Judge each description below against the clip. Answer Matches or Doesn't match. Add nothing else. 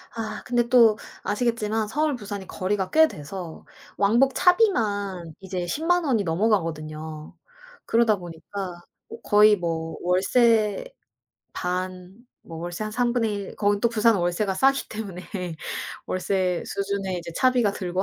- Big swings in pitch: Doesn't match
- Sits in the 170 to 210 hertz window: Matches